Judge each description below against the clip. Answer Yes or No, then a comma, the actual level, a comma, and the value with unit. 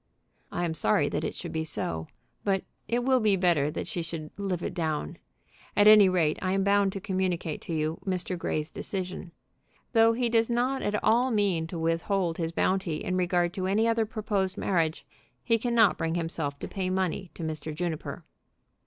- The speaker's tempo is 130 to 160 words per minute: No, average, 190 wpm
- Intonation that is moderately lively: Yes, average, 4.0 semitones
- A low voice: No, medium, 185 Hz